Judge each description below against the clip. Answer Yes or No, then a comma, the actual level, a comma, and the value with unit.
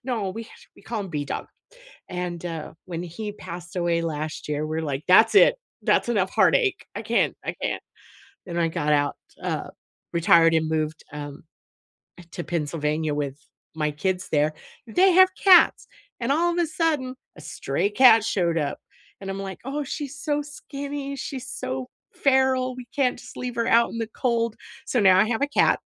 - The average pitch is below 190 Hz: No, high, 195 Hz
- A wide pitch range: Yes, wide, 8.3 semitones